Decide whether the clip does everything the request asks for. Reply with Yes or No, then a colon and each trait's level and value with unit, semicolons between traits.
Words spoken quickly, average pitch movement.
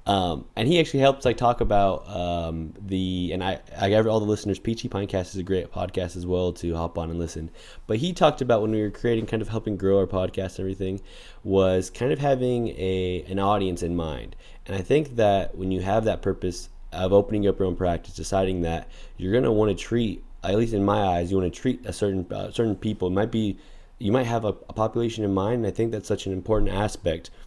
Yes: fast, 240 wpm; average, 3.3 semitones